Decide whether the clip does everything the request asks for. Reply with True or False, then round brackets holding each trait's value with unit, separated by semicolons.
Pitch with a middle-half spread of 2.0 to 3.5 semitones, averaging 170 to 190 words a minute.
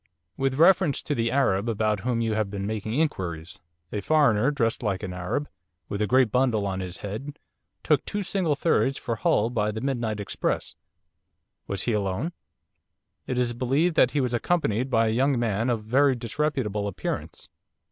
False (4.6 semitones; 180 wpm)